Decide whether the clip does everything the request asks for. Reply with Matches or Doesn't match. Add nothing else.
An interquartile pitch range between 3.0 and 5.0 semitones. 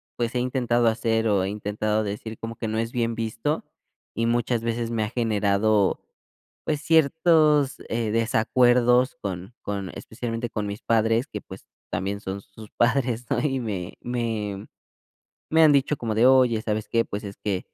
Doesn't match